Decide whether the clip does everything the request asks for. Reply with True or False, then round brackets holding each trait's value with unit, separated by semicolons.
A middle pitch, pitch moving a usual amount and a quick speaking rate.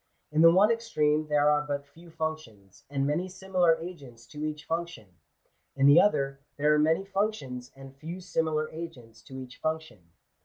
False (155 Hz; 3.5 semitones; 170 wpm)